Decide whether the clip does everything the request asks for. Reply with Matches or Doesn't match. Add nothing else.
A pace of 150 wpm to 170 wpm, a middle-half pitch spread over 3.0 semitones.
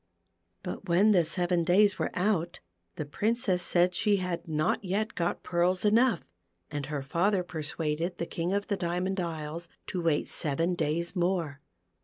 Doesn't match